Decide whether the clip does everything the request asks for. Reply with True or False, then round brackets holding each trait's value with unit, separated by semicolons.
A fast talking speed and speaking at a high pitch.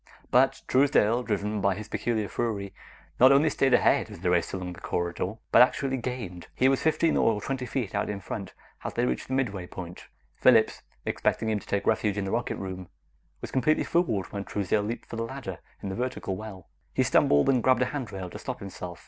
False (210 wpm; 105 Hz)